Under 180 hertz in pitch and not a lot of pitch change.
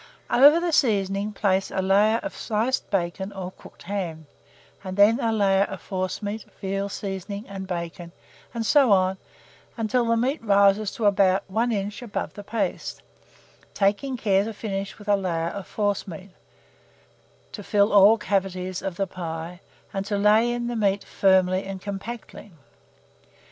No: high, 200 Hz; narrow, 2.3 semitones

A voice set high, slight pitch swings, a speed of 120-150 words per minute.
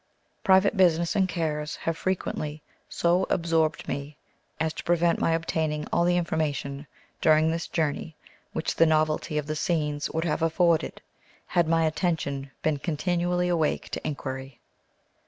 No: medium, 160 Hz; narrow, 2.2 semitones; average, 145 wpm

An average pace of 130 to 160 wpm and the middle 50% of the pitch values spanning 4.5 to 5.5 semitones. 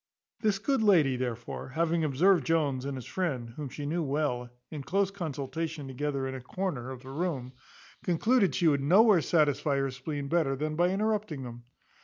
No: average, 180 wpm; average, 4.8 semitones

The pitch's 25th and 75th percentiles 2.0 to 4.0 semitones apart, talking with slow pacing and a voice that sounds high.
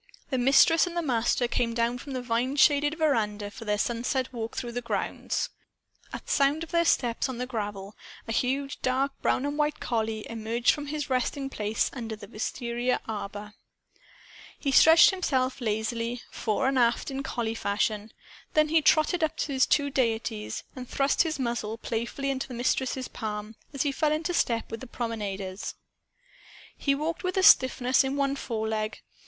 No: average, 3.7 semitones; average, 175 wpm; very high, 250 Hz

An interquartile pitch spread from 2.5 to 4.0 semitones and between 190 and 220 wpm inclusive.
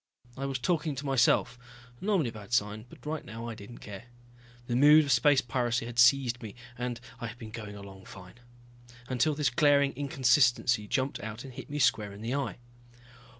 Yes: average, 3.5 semitones; average, 195 wpm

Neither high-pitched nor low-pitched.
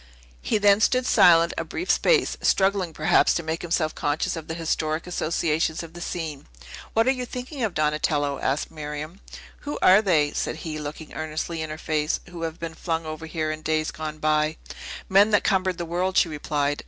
Yes: medium, 160 Hz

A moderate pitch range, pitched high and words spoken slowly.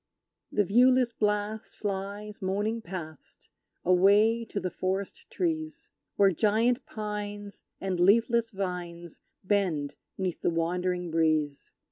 Yes: average, 3.3 semitones; high, 200 Hz; slow, 110 wpm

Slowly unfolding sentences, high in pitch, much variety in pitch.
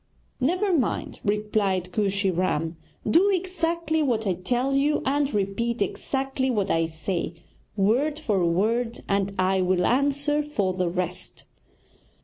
Yes: slow, 130 wpm; high, 215 Hz; wide, 7.1 semitones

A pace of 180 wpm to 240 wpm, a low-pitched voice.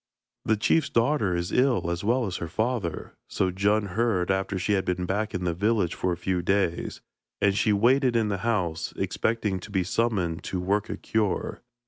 Yes: average, 195 wpm; low, 100 Hz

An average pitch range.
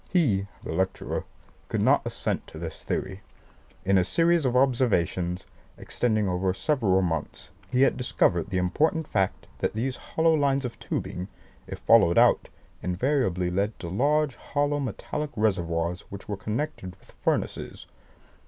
No: wide, 6.9 semitones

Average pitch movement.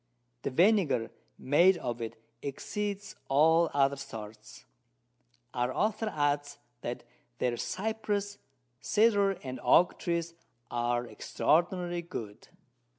No: wide, 7.6 semitones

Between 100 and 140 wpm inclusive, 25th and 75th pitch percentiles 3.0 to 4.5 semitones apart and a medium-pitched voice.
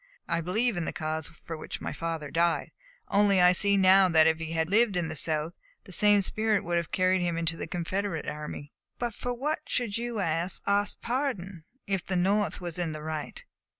No: fast, 205 wpm; average, 3.8 semitones; medium, 180 Hz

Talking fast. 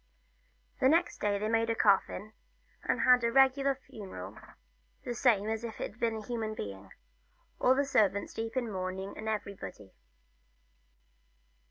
No: average, 145 wpm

